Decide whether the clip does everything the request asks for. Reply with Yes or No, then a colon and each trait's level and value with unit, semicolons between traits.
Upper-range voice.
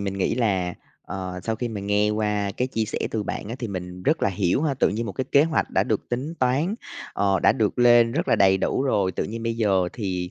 No: low, 105 Hz